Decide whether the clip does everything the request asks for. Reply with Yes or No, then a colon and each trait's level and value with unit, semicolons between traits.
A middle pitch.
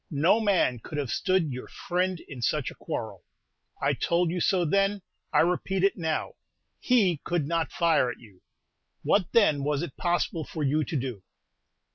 Yes: medium, 165 Hz